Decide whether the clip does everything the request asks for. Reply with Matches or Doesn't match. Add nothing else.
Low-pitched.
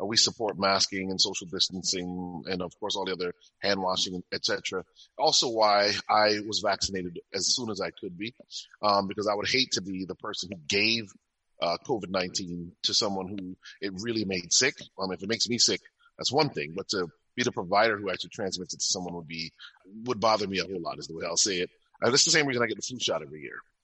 Matches